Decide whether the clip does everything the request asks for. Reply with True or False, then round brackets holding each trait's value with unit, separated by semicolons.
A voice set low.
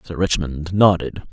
True (85 Hz)